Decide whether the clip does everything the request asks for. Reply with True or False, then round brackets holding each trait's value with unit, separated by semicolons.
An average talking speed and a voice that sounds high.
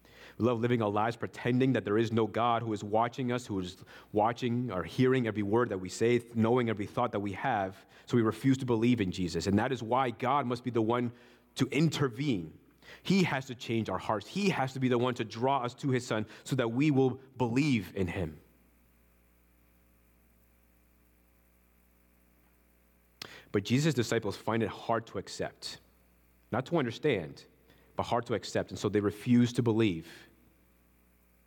False (180 wpm; 110 Hz)